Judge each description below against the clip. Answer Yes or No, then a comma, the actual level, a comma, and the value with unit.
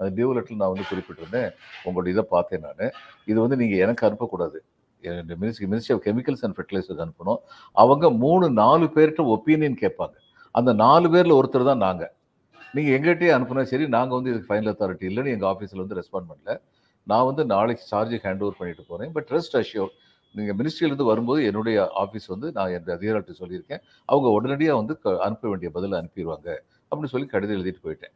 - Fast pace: Yes, fast, 175 wpm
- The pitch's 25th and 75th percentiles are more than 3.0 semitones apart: Yes, wide, 5.6 semitones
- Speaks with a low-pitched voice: Yes, low, 110 Hz